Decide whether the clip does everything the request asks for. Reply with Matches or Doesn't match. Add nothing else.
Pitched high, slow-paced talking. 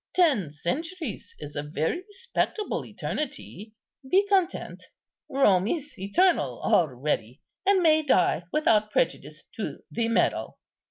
Matches